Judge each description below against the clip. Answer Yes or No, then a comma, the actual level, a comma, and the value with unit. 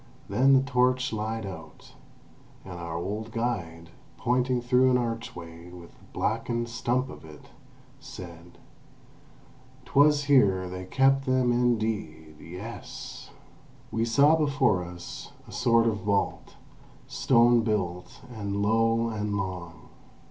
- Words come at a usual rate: No, slow, 120 wpm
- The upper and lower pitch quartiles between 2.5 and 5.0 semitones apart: No, wide, 5.4 semitones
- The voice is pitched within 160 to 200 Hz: No, low, 110 Hz